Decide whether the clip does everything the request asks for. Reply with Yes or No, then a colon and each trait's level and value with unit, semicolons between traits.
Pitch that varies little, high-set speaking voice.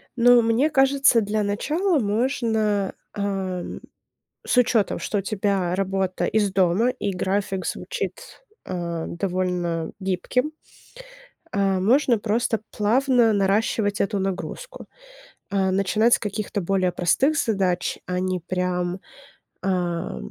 No: average, 3.6 semitones; high, 200 Hz